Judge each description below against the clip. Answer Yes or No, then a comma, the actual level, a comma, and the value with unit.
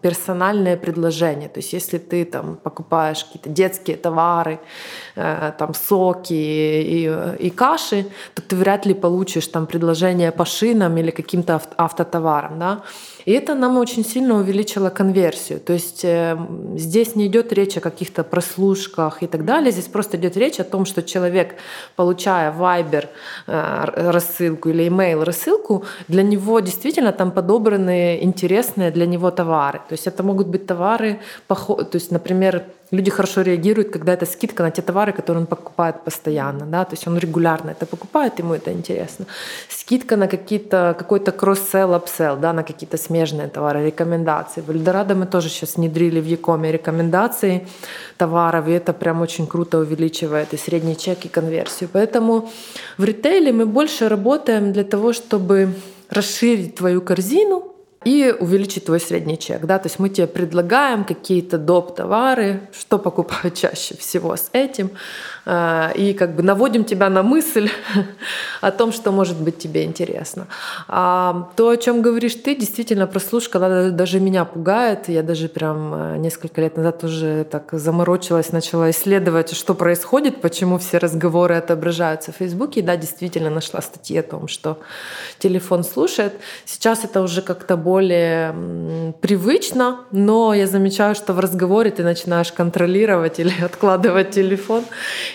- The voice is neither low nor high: Yes, medium, 180 Hz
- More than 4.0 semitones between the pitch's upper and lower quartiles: No, average, 3.1 semitones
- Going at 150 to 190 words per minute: Yes, average, 155 wpm